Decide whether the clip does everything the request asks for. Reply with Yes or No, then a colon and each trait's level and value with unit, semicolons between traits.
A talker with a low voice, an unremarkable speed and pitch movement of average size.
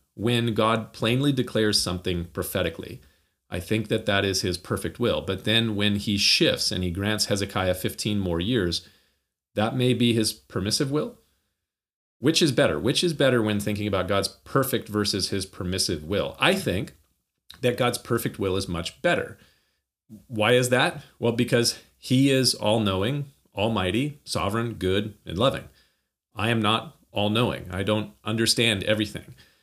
Yes: low, 105 Hz; average, 160 wpm; average, 3.5 semitones